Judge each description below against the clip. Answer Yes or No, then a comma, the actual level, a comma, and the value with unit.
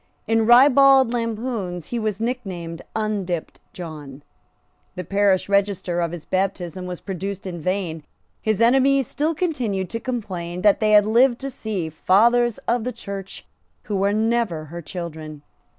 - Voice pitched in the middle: No, high, 200 Hz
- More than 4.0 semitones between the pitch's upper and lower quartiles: Yes, average, 4.9 semitones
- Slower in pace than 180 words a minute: Yes, average, 150 wpm